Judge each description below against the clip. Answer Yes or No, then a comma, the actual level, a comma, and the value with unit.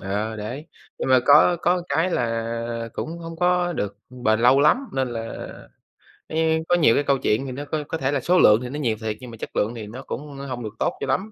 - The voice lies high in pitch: No, low, 135 Hz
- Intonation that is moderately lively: No, wide, 5.7 semitones